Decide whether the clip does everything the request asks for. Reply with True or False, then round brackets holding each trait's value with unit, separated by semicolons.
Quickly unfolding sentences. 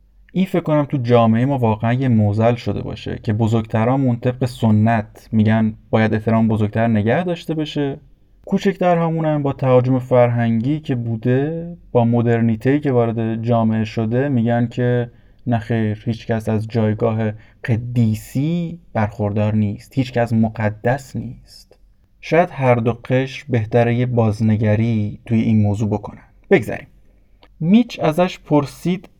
False (135 wpm)